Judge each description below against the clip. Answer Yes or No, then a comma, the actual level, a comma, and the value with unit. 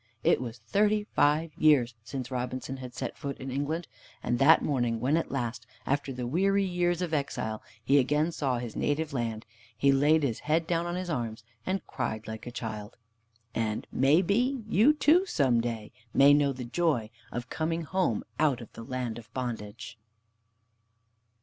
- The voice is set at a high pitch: No, low, 135 Hz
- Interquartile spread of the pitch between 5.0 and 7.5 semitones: Yes, wide, 5.4 semitones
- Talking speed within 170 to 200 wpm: Yes, average, 175 wpm